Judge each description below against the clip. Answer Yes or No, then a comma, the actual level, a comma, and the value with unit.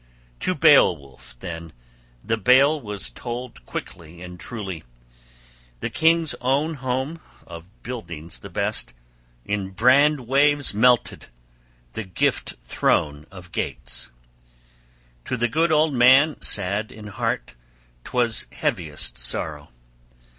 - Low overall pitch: Yes, low, 110 Hz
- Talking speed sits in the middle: No, slow, 110 wpm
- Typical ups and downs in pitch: No, wide, 7.6 semitones